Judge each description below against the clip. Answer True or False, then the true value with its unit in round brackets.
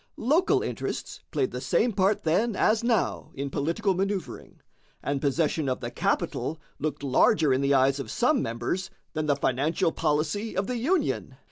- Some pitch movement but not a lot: False (7.2 semitones)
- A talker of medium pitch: True (165 Hz)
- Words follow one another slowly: False (165 wpm)